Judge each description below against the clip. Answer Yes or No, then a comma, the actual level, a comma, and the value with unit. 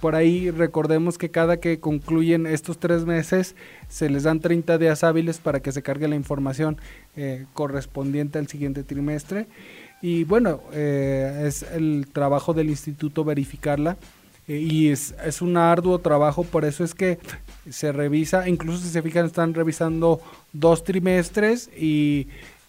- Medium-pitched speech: Yes, medium, 160 Hz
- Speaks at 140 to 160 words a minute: Yes, average, 155 wpm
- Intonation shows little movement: Yes, narrow, 2.3 semitones